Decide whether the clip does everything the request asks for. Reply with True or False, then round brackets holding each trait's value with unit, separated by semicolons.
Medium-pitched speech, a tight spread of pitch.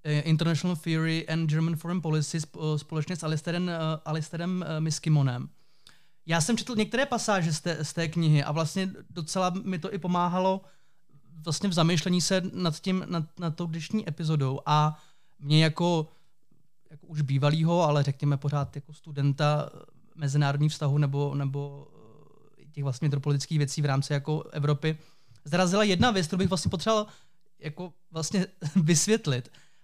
False (160 Hz; 3.1 semitones)